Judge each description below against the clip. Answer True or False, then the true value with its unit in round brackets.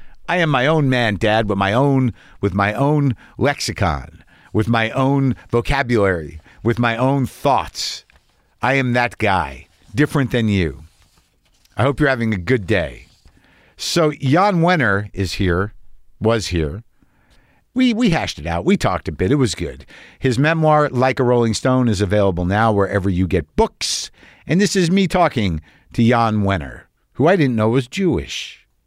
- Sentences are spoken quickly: False (170 wpm)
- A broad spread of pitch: True (5.8 semitones)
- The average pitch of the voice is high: False (115 Hz)